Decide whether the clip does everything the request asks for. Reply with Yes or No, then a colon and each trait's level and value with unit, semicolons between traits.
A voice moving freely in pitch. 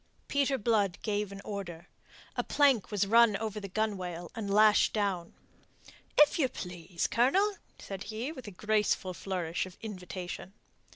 No: average, 3.4 semitones